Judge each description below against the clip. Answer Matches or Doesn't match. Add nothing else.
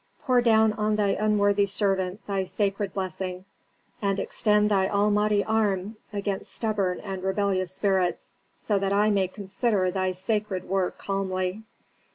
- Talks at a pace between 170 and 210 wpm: Doesn't match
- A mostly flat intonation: Matches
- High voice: Matches